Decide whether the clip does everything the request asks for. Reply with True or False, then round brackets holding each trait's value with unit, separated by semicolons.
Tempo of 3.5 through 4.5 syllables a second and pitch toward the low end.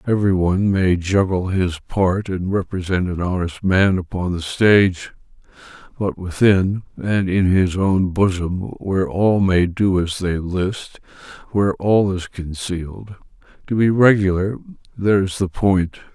True (4.2 syllables/s; 95 Hz)